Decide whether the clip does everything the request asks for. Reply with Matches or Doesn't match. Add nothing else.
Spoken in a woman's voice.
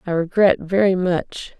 Matches